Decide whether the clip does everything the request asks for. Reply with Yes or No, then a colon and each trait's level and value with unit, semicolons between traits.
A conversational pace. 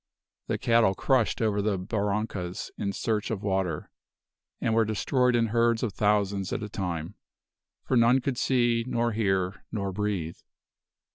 Yes: average, 150 wpm